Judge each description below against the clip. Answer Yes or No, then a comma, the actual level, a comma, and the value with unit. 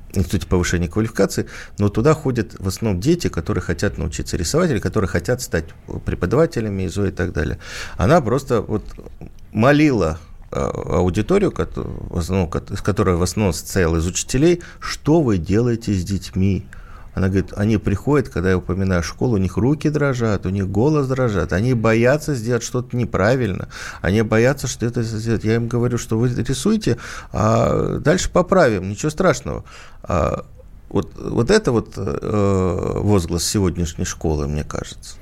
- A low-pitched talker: Yes, low, 100 Hz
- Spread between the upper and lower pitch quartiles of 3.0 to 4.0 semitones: No, average, 4.7 semitones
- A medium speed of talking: Yes, average, 145 wpm